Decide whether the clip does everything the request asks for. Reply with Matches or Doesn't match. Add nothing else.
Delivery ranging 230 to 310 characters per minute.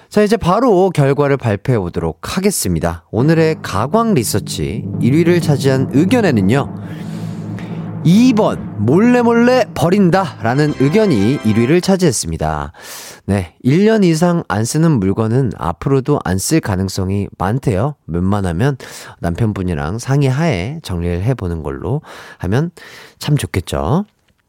Matches